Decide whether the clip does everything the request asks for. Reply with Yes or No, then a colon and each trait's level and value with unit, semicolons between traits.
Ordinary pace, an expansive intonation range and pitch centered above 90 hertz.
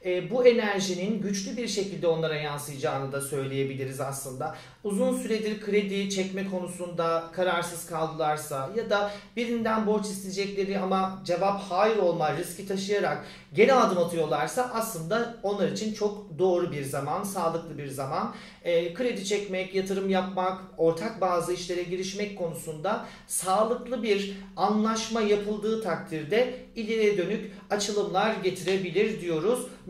No: average, 120 wpm; average, 3.9 semitones; high, 190 Hz